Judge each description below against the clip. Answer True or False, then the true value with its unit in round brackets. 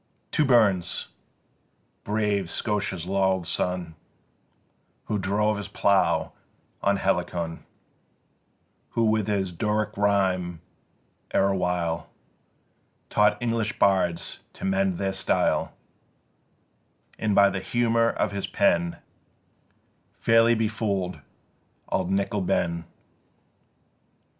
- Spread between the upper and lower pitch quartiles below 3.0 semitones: True (2.6 semitones)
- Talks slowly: True (90 wpm)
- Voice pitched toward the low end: True (100 Hz)